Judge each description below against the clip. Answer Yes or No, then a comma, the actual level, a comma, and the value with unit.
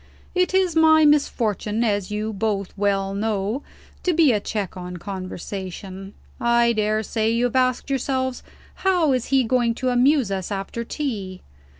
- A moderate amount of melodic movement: Yes, average, 4.7 semitones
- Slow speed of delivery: No, average, 160 wpm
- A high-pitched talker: Yes, high, 225 Hz